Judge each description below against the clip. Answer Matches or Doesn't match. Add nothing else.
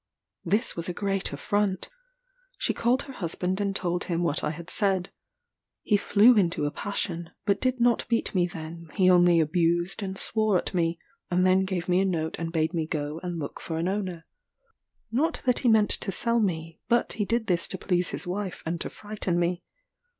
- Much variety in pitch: Doesn't match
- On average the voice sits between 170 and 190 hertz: Matches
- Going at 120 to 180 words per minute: Doesn't match